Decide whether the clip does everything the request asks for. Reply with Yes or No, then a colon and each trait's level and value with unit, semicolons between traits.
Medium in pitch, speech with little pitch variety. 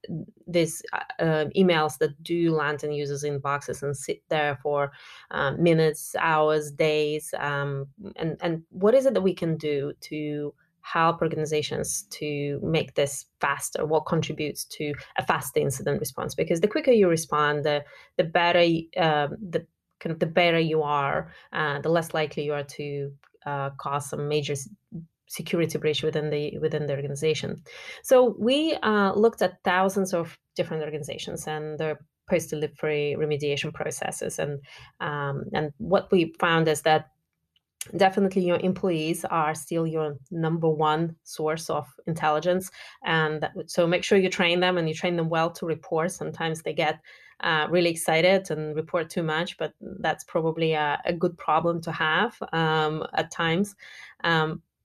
Yes: medium, 160 Hz; narrow, 2.3 semitones